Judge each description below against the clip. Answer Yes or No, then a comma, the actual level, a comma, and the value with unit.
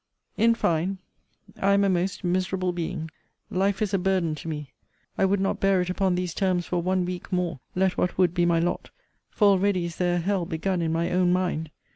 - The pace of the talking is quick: Yes, fast, 215 wpm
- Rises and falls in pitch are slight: Yes, narrow, 1.8 semitones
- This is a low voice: No, medium, 180 Hz